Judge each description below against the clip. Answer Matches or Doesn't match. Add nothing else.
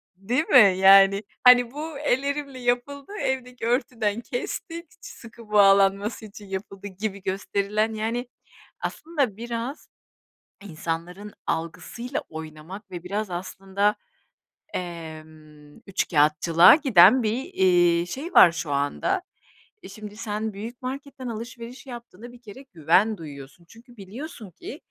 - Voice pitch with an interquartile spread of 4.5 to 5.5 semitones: Matches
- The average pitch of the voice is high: Matches